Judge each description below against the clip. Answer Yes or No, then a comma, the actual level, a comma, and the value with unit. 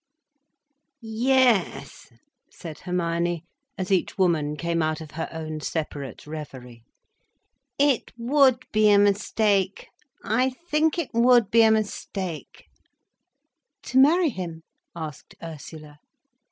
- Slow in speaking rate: Yes, slow, 105 wpm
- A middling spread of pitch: No, wide, 6.7 semitones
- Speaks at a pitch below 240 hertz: Yes, high, 190 Hz